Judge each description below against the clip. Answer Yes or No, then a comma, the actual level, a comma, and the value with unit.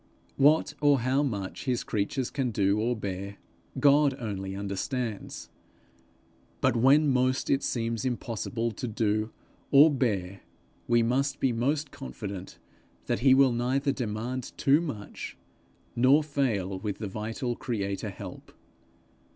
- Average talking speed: No, slow, 130 wpm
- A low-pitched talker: Yes, low, 120 Hz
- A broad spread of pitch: No, average, 4.6 semitones